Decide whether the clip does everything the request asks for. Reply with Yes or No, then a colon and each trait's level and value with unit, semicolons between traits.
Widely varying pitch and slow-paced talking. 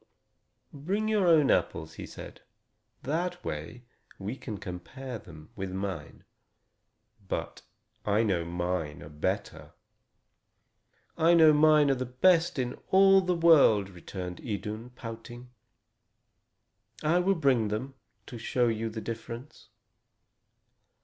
Yes: wide, 7.8 semitones; slow, 115 wpm